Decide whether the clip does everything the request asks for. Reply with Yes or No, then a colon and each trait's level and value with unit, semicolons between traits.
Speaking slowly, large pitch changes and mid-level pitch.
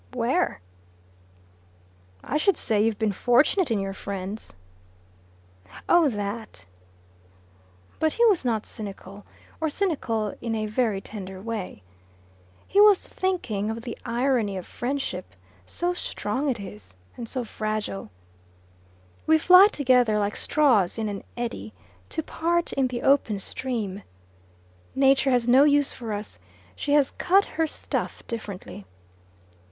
No: slow, 130 wpm; wide, 5.8 semitones; high, 235 Hz